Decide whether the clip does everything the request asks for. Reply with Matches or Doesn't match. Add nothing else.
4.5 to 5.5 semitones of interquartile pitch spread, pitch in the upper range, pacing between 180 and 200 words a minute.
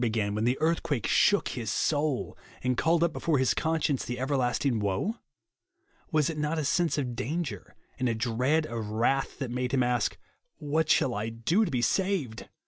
Doesn't match